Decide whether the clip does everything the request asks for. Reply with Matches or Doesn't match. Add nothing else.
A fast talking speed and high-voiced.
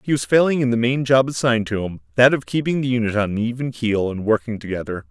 Doesn't match